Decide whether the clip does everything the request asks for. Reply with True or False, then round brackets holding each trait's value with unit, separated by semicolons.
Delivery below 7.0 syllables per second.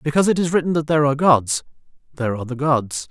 False (7.7 syllables/s)